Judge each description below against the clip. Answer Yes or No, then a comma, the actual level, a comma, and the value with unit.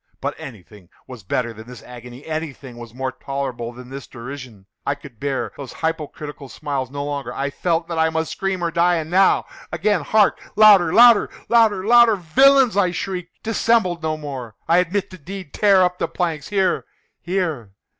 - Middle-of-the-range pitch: Yes, medium, 160 Hz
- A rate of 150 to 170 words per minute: Yes, average, 165 wpm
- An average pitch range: No, wide, 6.1 semitones